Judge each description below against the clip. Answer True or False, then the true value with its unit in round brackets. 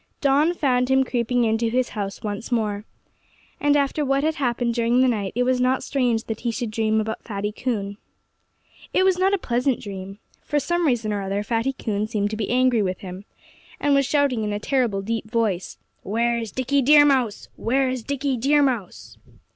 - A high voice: True (240 Hz)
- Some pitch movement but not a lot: True (4.0 semitones)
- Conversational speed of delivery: True (195 wpm)